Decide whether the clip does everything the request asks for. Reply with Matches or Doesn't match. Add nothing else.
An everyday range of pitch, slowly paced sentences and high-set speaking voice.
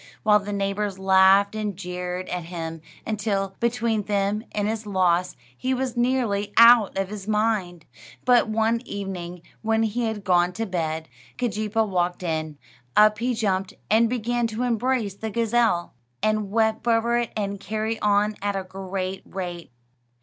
Doesn't match